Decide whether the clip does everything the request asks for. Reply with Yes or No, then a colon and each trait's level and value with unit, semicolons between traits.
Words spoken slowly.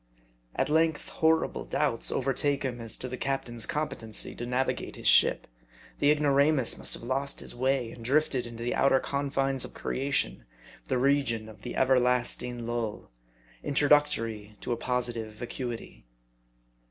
No: average, 150 wpm